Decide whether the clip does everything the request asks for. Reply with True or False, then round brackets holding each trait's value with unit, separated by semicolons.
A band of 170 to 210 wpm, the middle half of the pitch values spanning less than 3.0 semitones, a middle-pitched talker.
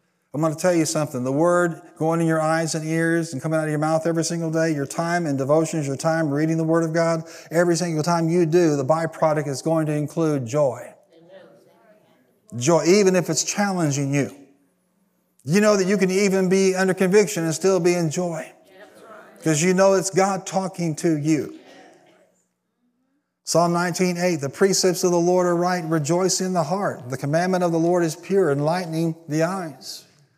True (190 wpm; 2.5 semitones; 165 Hz)